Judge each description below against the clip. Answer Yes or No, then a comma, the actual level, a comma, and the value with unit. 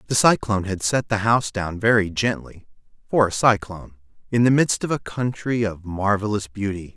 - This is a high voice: No, low, 105 Hz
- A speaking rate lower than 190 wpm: Yes, average, 165 wpm